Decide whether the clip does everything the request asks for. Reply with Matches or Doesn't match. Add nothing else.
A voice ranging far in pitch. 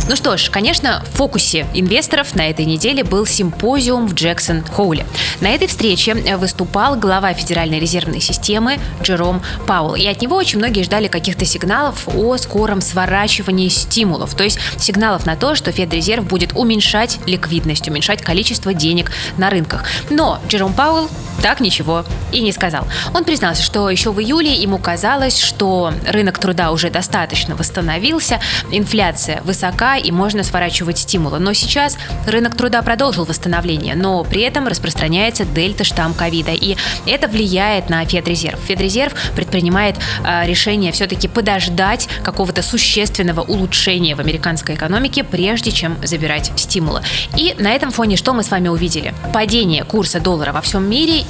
Doesn't match